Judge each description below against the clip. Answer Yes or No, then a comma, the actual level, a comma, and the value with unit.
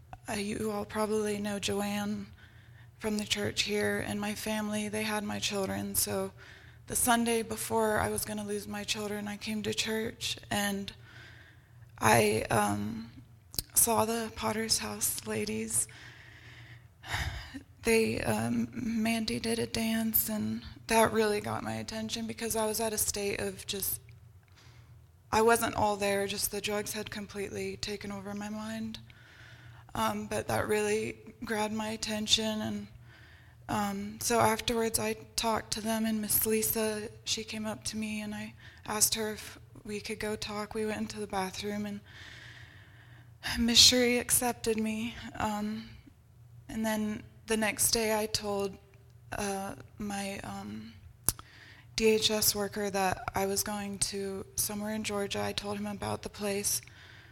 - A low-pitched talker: No, high, 200 Hz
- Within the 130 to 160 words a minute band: Yes, average, 145 wpm